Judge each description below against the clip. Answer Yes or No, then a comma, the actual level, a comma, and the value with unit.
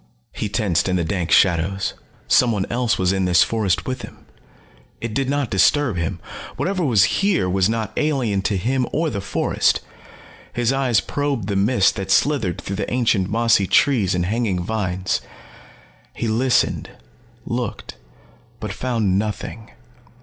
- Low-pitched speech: Yes, low, 110 Hz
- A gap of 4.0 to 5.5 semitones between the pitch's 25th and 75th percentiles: Yes, average, 4.6 semitones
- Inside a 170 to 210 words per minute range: No, average, 150 wpm